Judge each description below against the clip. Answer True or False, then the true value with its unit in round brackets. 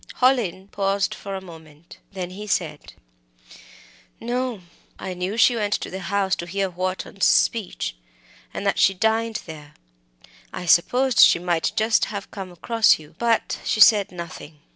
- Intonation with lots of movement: False (3.8 semitones)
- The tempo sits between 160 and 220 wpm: False (150 wpm)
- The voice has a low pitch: False (195 Hz)